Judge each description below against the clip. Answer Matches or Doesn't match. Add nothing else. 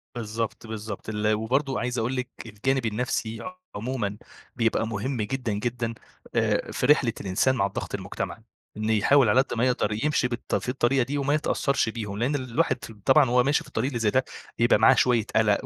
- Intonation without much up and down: Doesn't match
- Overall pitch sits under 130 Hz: Matches